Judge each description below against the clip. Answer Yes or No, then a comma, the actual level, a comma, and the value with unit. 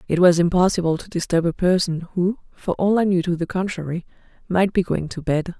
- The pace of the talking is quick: Yes, fast, 215 wpm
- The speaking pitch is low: No, medium, 175 Hz